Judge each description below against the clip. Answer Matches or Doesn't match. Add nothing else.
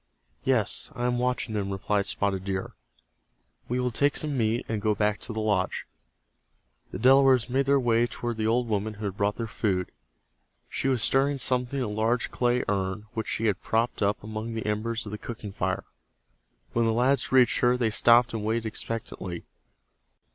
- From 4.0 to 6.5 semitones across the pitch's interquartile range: Doesn't match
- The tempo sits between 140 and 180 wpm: Doesn't match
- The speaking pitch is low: Matches